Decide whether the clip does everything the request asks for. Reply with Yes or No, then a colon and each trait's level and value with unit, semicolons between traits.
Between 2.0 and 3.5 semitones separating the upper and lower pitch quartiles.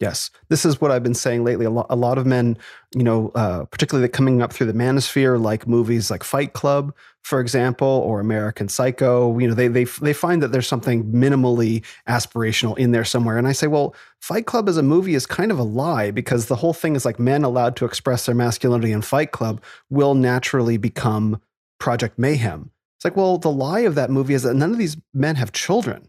Yes: average, 2.8 semitones